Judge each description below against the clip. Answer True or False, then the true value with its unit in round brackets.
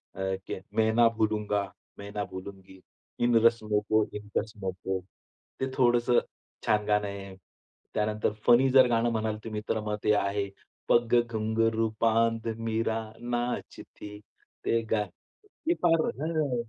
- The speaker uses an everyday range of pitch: False (2.2 semitones)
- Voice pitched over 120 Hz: False (110 Hz)